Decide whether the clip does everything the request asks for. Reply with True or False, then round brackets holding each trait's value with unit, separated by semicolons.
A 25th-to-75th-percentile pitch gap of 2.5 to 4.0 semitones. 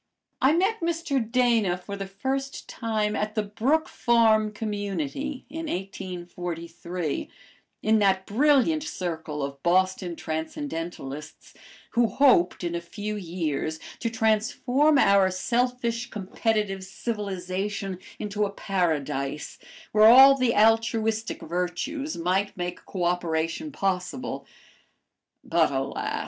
False (5.0 semitones)